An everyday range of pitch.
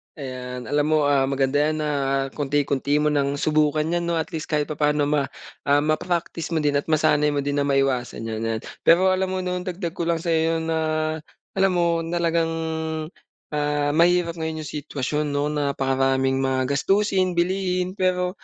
Yes: average, 3.2 semitones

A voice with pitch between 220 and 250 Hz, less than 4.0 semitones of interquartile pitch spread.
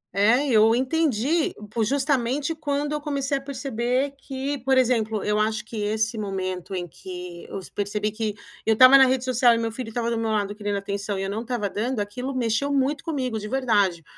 No: high, 230 Hz; average, 4.3 semitones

